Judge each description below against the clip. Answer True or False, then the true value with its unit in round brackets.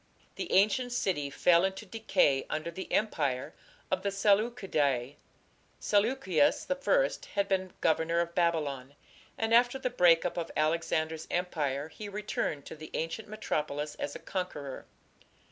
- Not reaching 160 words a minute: True (140 wpm)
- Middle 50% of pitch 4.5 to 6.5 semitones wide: True (5.3 semitones)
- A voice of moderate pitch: True (170 Hz)